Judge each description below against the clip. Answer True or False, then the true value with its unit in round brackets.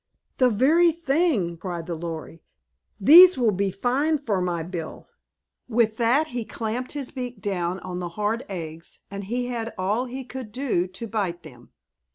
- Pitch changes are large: True (6.0 semitones)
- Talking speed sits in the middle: True (170 wpm)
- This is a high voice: True (220 Hz)